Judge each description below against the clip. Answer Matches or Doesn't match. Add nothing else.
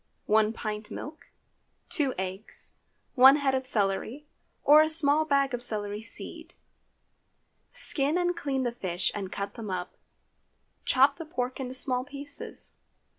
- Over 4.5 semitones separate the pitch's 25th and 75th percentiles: Matches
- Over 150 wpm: Doesn't match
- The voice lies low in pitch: Doesn't match